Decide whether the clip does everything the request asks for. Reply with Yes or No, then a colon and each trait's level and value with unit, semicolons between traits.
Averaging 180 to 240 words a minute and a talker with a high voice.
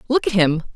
Yes: fast, 235 wpm; high, 220 Hz